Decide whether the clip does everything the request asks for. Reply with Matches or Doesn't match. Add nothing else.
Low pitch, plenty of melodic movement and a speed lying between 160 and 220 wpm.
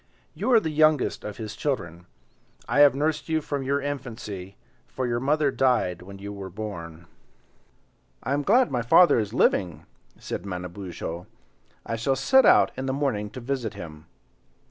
Matches